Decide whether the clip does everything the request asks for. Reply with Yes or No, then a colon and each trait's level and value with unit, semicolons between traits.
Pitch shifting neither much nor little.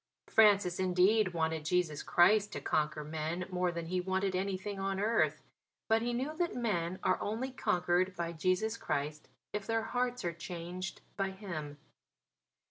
Yes: average, 3.6 semitones